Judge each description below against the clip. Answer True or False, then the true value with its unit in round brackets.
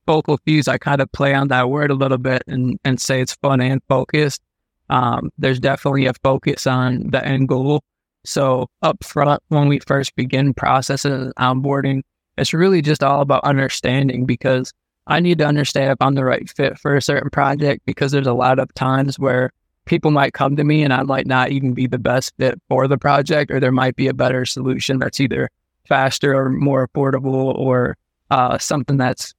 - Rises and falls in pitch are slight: True (1.6 semitones)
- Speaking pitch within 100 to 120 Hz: False (135 Hz)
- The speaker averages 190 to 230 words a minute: True (200 wpm)